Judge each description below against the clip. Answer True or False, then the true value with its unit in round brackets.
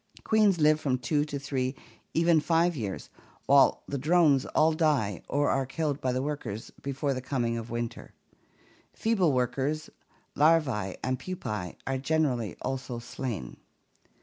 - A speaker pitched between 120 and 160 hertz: True (135 Hz)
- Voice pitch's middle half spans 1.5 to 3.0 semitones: False (3.7 semitones)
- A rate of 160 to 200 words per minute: False (145 wpm)